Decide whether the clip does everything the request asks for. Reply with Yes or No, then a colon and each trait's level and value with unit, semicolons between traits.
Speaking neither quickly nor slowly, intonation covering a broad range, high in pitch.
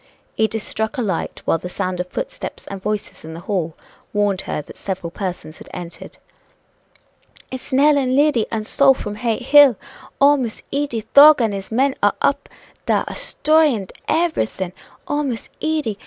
Yes: average, 170 wpm; wide, 6.7 semitones; high, 225 Hz